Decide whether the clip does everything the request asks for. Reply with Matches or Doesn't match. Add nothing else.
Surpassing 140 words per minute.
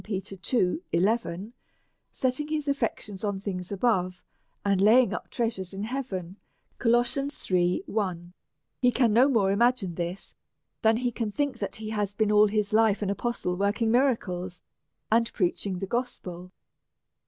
Doesn't match